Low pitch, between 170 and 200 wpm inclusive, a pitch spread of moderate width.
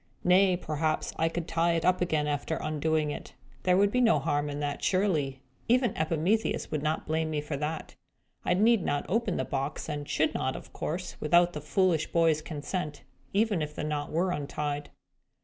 No: medium, 160 Hz; average, 190 wpm; average, 3.4 semitones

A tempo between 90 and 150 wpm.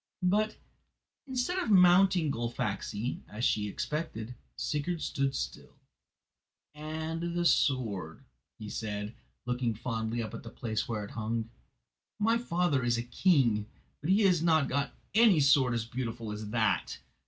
Yes: average, 140 wpm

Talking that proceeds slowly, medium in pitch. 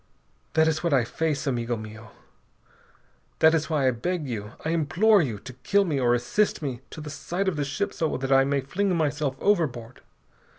No: average, 200 wpm; medium, 145 Hz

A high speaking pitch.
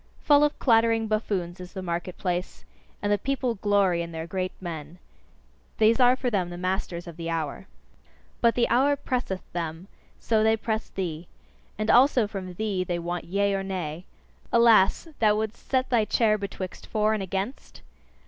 Yes: high, 200 Hz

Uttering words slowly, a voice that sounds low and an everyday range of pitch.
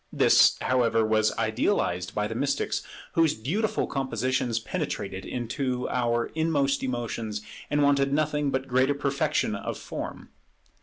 Yes: slow, 125 wpm; low, 130 Hz; average, 3.9 semitones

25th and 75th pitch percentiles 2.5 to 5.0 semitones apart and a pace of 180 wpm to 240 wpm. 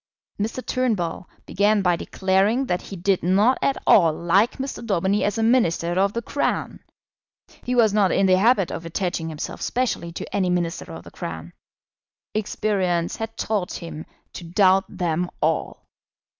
No: average, 3.9 semitones; average, 160 wpm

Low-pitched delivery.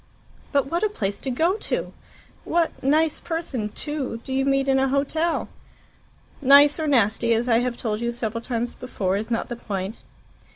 No: very high, 260 Hz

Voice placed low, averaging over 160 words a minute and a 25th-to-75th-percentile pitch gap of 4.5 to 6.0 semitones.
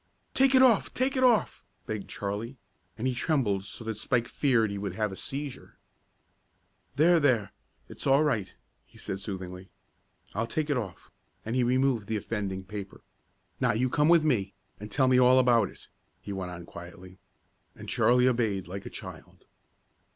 Yes: low, 115 Hz; average, 175 wpm; average, 5.3 semitones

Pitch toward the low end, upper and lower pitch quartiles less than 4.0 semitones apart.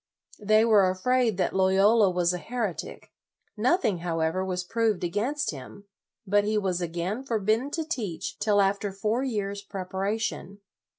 No: high, 200 Hz; average, 3.3 semitones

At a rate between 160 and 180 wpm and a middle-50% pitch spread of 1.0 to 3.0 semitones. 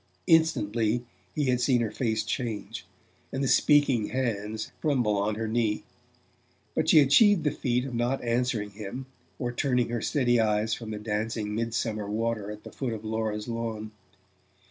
Yes: average, 165 wpm; average, 2.7 semitones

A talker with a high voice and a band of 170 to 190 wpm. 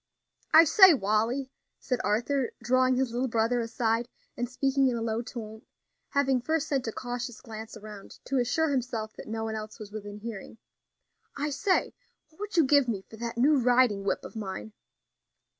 Yes: high, 240 Hz; average, 180 wpm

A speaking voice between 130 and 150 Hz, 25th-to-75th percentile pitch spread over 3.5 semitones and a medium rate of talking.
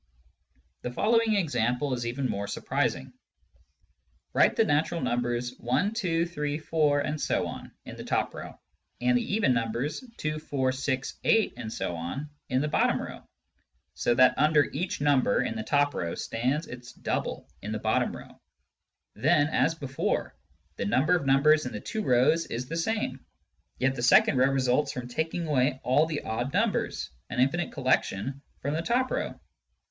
Yes: medium, 140 Hz; average, 4.1 semitones; average, 165 wpm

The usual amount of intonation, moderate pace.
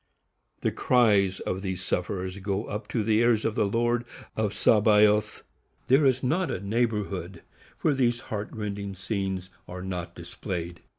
Yes: average, 3.5 semitones; average, 155 wpm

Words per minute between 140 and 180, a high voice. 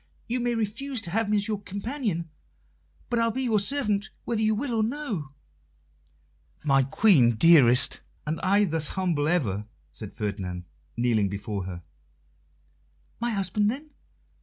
Yes: average, 145 wpm; high, 195 Hz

